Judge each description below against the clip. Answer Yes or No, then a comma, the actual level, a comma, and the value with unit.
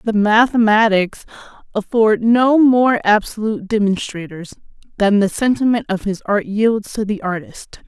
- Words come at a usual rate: No, slow, 130 wpm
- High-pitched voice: Yes, high, 215 Hz